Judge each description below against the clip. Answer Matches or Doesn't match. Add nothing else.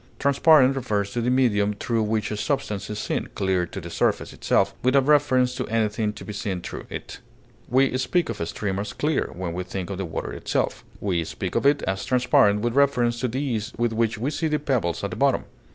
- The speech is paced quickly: Matches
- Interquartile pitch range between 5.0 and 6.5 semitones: Doesn't match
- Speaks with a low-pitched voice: Matches